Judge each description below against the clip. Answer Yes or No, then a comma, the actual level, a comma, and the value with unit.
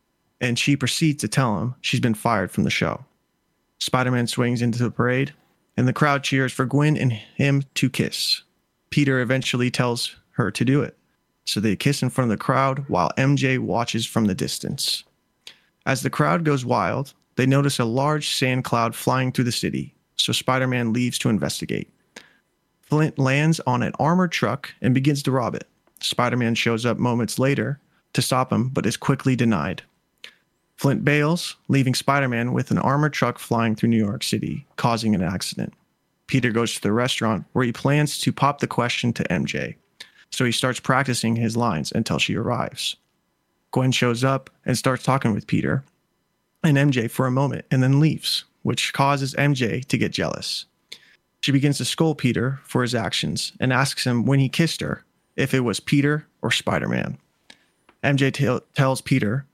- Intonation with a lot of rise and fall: No, narrow, 2.6 semitones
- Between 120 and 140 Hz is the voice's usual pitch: Yes, low, 130 Hz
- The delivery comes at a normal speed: Yes, average, 185 wpm